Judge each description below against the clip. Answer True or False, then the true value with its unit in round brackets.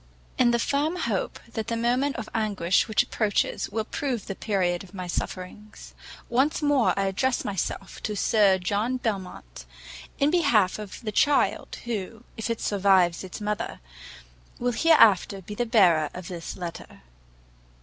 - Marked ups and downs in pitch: False (4.1 semitones)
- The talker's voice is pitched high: True (210 Hz)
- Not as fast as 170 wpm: True (155 wpm)